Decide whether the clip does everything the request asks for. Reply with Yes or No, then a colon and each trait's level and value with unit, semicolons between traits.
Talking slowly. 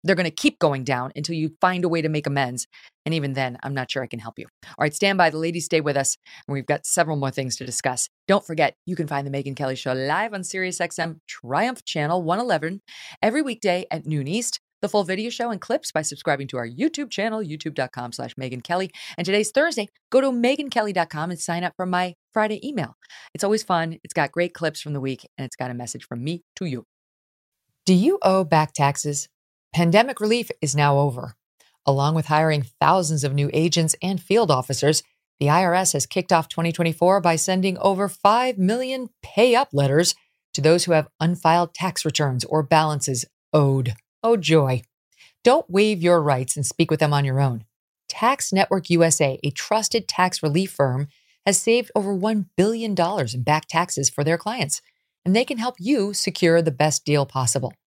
No: fast, 205 wpm